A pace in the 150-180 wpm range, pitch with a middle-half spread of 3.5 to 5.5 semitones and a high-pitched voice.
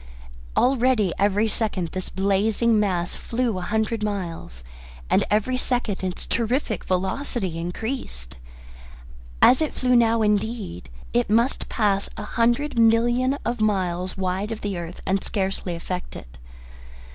No: slow, 135 wpm; average, 4.0 semitones; high, 210 Hz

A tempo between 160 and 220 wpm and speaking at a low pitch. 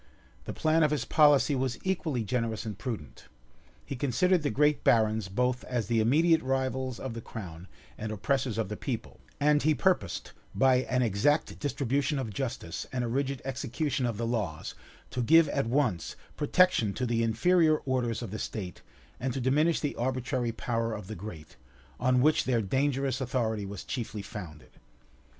Yes: average, 170 wpm; low, 125 Hz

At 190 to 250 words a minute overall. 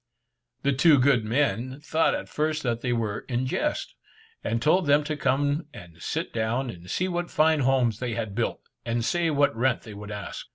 Yes: average, 200 wpm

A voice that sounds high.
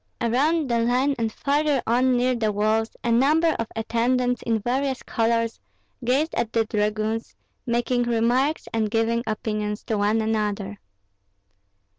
Yes: high, 230 Hz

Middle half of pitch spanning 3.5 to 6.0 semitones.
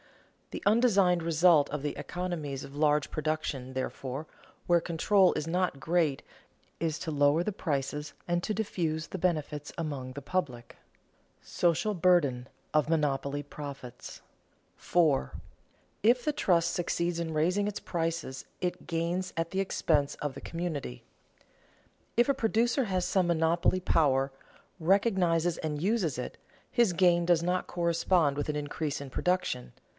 Yes: average, 3.8 semitones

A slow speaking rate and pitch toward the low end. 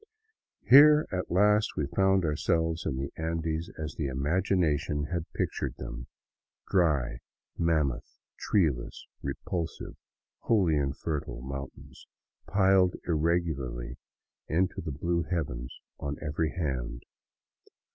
Yes: slow, 105 wpm; very low, 80 Hz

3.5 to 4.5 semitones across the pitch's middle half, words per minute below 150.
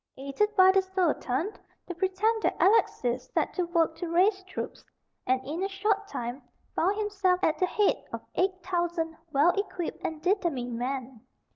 No: average, 4.2 semitones; average, 160 wpm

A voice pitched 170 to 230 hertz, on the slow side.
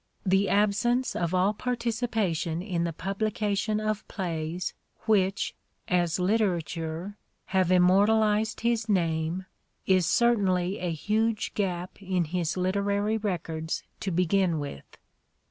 Yes: high, 190 Hz; slow, 115 wpm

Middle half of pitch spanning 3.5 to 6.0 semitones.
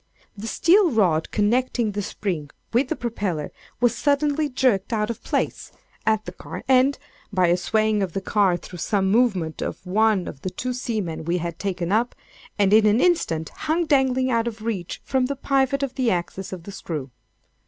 Yes: wide, 5.5 semitones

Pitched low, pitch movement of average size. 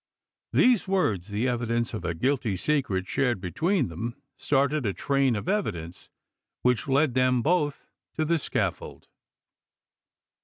No: low, 125 Hz; wide, 6.2 semitones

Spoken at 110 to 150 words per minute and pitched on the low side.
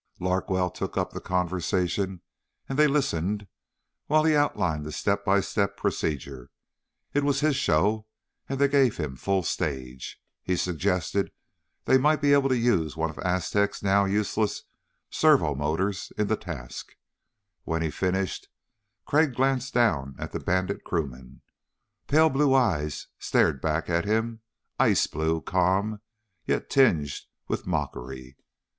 Yes: average, 140 wpm; very low, 95 Hz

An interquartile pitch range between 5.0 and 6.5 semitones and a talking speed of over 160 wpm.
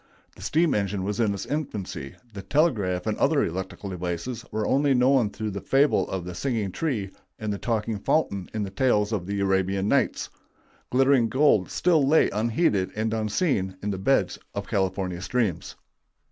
Yes: average, 5.3 semitones; average, 175 wpm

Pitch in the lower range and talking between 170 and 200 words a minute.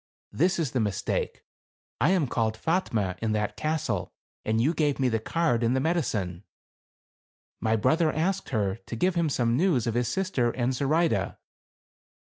Yes: low, 130 Hz; average, 175 wpm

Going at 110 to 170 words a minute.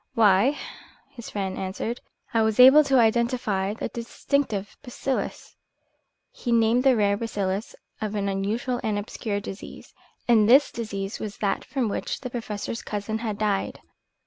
Yes: average, 150 wpm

